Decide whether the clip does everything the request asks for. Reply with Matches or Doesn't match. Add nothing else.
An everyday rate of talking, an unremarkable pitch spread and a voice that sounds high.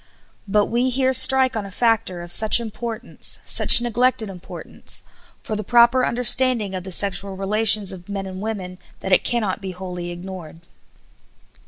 Matches